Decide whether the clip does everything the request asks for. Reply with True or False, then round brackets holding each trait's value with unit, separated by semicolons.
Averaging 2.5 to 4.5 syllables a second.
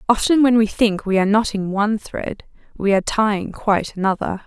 False (5.8 syllables/s)